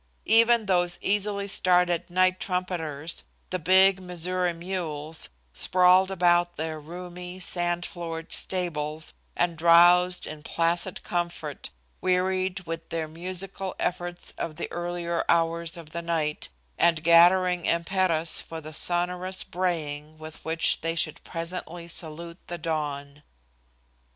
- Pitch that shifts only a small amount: Yes, narrow, 1.9 semitones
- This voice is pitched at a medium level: Yes, medium, 175 Hz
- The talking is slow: Yes, slow, 120 wpm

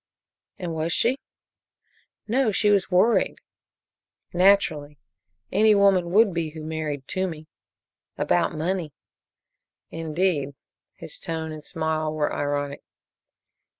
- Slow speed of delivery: Yes, slow, 105 wpm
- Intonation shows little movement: No, average, 3.8 semitones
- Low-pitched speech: No, medium, 165 Hz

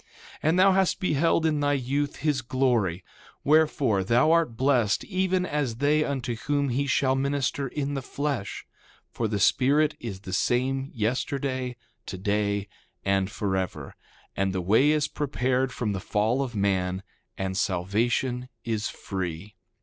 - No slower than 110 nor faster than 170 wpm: Yes, average, 150 wpm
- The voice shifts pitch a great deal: Yes, wide, 5.8 semitones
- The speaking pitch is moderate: No, low, 125 Hz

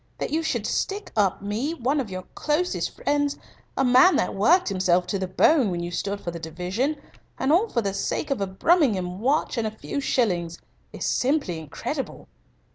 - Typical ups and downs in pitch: No, wide, 7.7 semitones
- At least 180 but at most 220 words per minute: Yes, average, 195 wpm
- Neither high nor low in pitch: No, high, 220 Hz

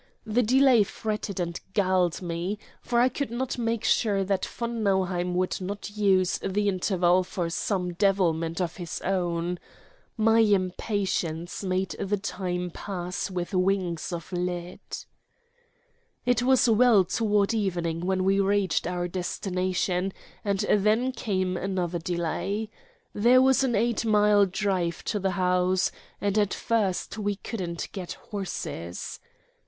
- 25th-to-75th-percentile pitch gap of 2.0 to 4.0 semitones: Yes, average, 2.8 semitones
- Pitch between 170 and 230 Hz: Yes, high, 190 Hz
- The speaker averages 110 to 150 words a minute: Yes, slow, 135 wpm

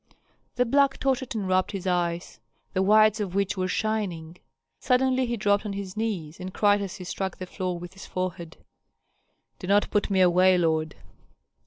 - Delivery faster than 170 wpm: Yes, average, 180 wpm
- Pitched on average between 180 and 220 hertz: Yes, high, 190 Hz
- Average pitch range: Yes, average, 3.0 semitones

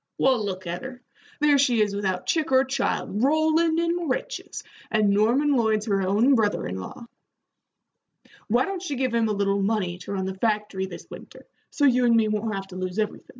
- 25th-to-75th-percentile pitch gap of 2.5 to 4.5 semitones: No, average, 5.2 semitones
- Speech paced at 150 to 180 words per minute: No, average, 200 wpm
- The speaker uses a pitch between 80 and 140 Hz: No, high, 220 Hz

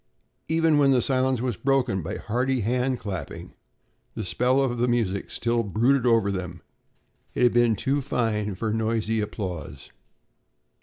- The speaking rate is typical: Yes, average, 150 wpm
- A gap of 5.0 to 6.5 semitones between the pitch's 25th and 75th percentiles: No, average, 3.6 semitones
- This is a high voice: No, low, 115 Hz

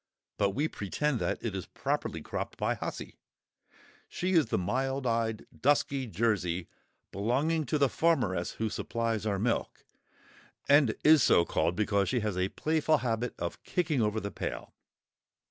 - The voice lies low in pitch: Yes, low, 115 Hz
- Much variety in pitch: Yes, wide, 5.9 semitones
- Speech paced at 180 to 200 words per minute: No, average, 155 wpm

